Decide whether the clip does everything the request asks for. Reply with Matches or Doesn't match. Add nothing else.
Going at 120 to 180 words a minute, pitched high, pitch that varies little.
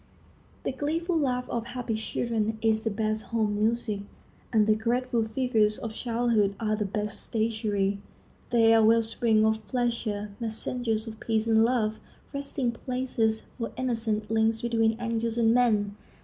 Matches